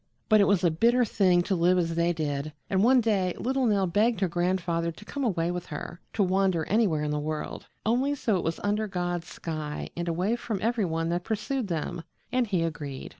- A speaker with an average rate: No, fast, 220 wpm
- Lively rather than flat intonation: No, average, 4.3 semitones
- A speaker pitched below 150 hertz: No, medium, 180 Hz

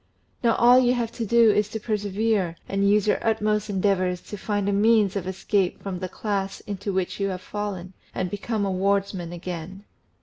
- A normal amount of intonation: No, narrow, 2.1 semitones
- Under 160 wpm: No, average, 195 wpm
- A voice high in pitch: Yes, high, 200 Hz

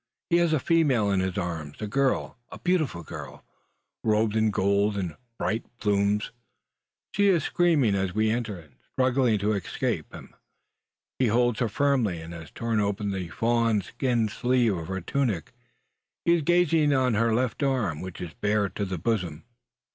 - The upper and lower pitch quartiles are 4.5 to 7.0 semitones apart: Yes, average, 4.8 semitones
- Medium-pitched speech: No, low, 110 Hz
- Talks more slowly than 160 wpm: No, average, 170 wpm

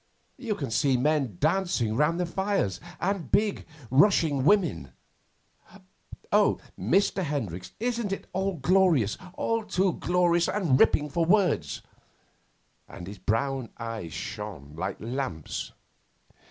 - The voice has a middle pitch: Yes, medium, 150 Hz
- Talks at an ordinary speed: No, slow, 120 wpm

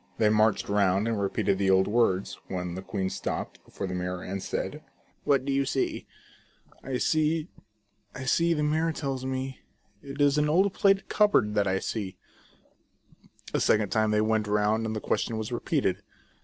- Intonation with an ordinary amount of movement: No, wide, 5.8 semitones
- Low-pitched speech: Yes, low, 110 Hz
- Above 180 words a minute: Yes, average, 190 wpm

